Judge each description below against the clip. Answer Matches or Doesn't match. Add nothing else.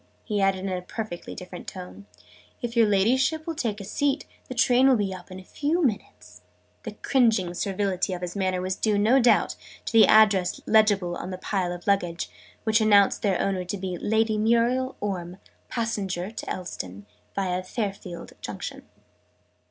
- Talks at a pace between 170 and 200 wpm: Matches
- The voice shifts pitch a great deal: Doesn't match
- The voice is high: Matches